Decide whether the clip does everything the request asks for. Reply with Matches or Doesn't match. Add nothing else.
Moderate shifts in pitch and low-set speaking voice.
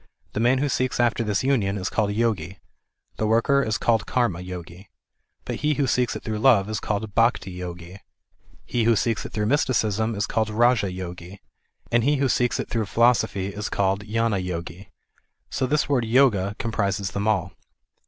Matches